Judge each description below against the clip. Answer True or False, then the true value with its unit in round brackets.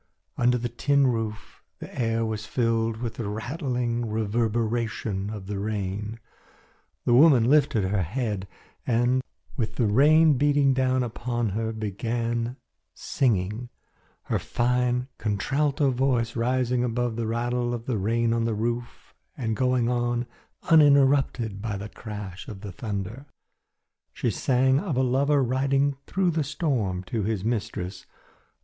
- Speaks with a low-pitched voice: True (120 Hz)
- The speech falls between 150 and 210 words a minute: False (140 wpm)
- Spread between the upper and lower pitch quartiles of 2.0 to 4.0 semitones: True (2.9 semitones)